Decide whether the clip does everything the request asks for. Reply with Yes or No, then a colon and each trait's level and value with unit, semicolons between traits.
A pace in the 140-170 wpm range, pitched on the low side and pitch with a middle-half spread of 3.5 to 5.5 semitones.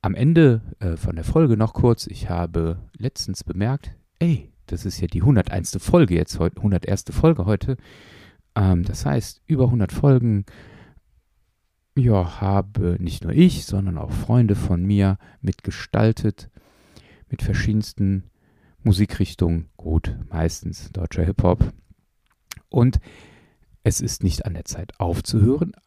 No: slow, 125 wpm; low, 100 Hz; average, 4.5 semitones